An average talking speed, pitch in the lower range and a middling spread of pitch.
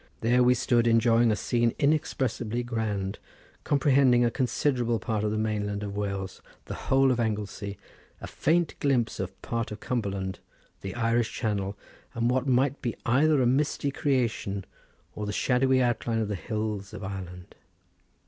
Yes: average, 160 wpm; low, 115 Hz; average, 3.4 semitones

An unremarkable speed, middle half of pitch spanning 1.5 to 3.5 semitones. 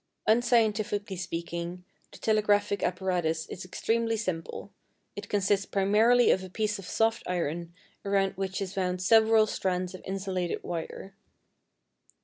No: slow, 130 wpm; average, 2.8 semitones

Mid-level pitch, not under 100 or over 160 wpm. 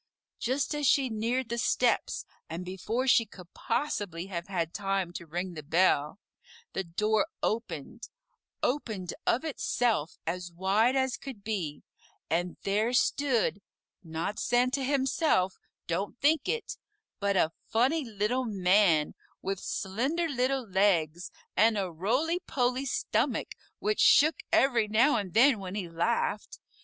No: high, 210 Hz; slow, 135 wpm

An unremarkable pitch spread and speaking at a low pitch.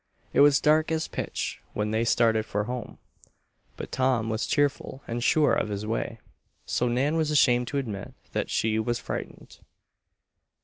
Yes: average, 4.3 semitones; low, 120 Hz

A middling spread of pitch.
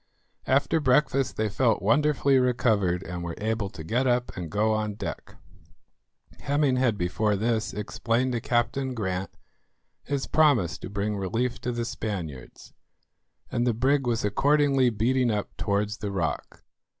Yes: average, 4.1 semitones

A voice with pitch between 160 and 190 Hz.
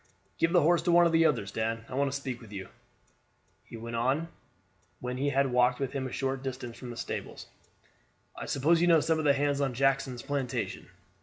No: low, 135 Hz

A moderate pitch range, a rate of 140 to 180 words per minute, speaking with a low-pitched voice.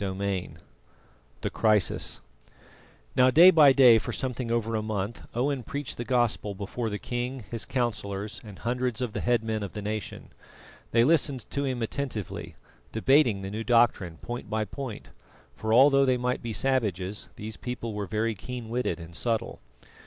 Yes: average, 3.1 semitones; average, 170 wpm; low, 115 Hz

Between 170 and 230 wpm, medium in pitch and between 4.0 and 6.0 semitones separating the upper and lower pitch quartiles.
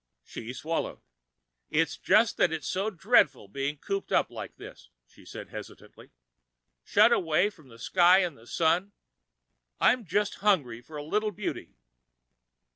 No: average, 145 wpm; medium, 165 Hz; average, 5.2 semitones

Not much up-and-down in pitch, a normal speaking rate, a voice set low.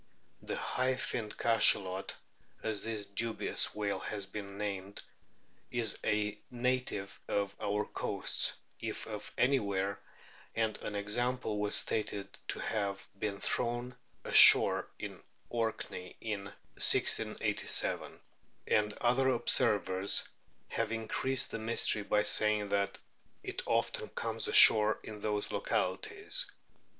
No: narrow, 2.3 semitones; slow, 115 wpm; low, 105 Hz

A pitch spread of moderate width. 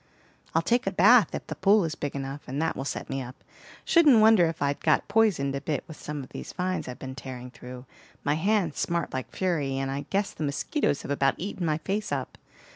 No: wide, 6.0 semitones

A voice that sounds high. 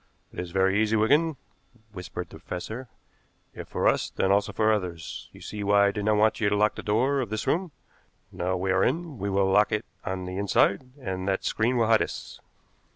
No: low, 105 Hz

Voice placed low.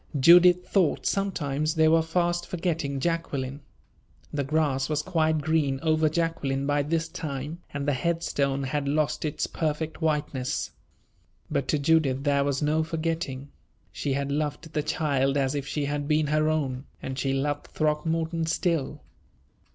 No: medium, 150 Hz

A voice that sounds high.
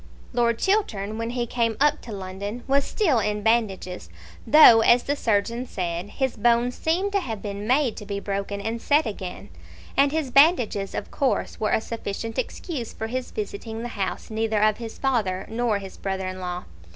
Yes: high, 225 Hz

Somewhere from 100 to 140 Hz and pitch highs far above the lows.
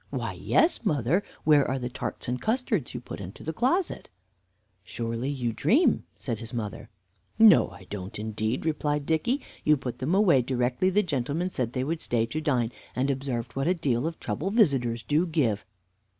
Yes: low, 135 Hz; wide, 5.9 semitones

